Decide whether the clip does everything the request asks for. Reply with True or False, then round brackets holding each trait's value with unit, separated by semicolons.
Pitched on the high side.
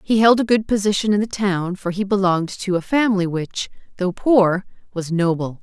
True (195 Hz)